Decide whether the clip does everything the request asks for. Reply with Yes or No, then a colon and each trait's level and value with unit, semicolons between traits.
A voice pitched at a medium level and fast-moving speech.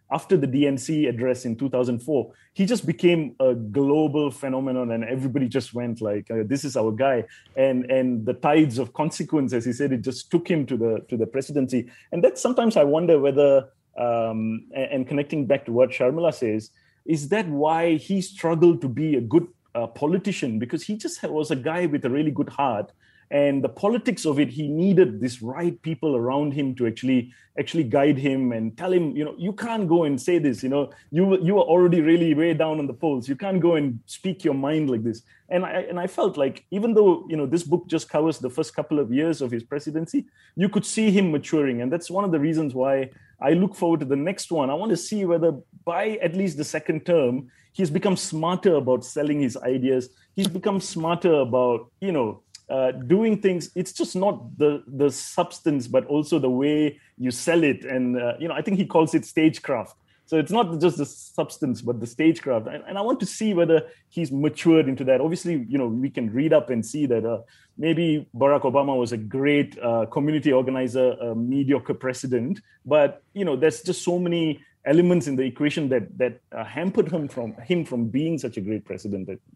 Yes: medium, 145 Hz; fast, 215 wpm